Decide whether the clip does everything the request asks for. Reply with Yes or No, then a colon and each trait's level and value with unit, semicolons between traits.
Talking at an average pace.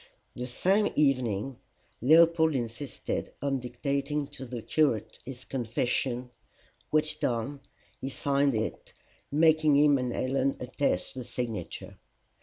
No: slow, 115 wpm